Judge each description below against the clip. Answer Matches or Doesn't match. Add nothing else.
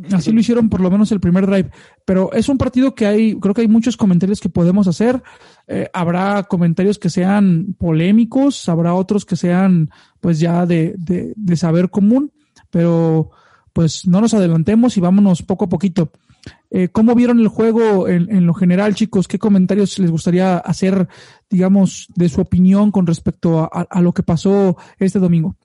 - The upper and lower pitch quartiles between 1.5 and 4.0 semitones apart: Matches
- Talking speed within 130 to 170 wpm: Doesn't match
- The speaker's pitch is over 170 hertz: Matches